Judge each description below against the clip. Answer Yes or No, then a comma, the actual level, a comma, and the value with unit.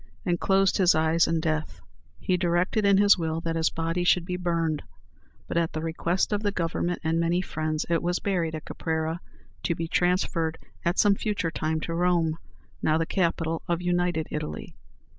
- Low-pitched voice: No, medium, 170 Hz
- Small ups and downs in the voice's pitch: Yes, narrow, 1.8 semitones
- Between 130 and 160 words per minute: No, average, 185 wpm